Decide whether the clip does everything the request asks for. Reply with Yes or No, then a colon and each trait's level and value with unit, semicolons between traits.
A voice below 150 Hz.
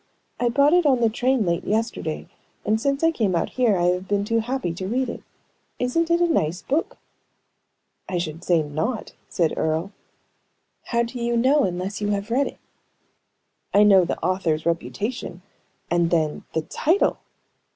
No: high, 210 Hz